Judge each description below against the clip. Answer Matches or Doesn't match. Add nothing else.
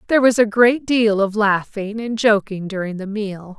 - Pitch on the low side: Doesn't match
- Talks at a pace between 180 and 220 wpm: Matches